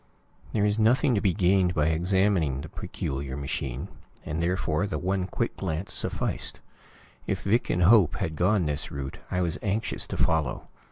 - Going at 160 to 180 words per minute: Yes, average, 170 wpm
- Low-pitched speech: Yes, very low, 90 Hz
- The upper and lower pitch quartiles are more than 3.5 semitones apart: Yes, average, 4.6 semitones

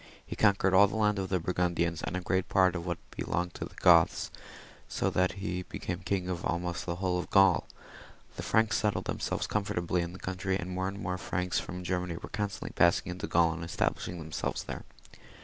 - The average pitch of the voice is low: Yes, very low, 90 Hz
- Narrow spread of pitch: Yes, narrow, 1.6 semitones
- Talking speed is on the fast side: Yes, fast, 215 wpm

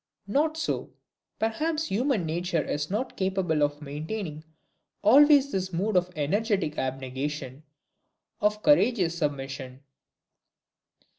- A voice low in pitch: No, medium, 180 Hz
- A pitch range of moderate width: No, wide, 7.0 semitones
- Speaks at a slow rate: Yes, slow, 100 wpm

